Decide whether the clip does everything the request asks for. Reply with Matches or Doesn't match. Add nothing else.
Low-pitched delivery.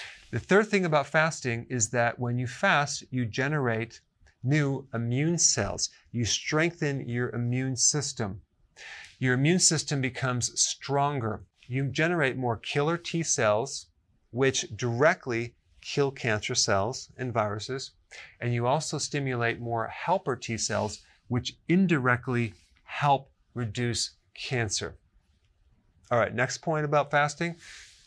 Matches